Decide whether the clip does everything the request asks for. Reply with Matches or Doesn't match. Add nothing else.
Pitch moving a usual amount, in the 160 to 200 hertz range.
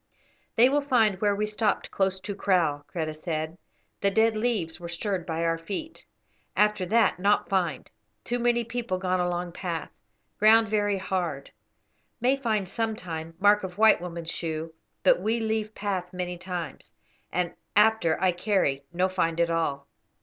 Matches